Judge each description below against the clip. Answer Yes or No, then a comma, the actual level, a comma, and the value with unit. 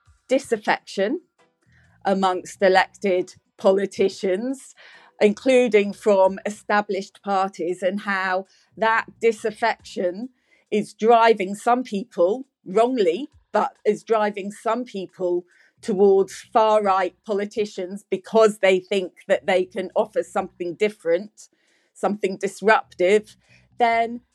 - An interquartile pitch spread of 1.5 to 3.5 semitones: Yes, average, 3.0 semitones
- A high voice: Yes, high, 205 Hz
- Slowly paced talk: Yes, slow, 95 wpm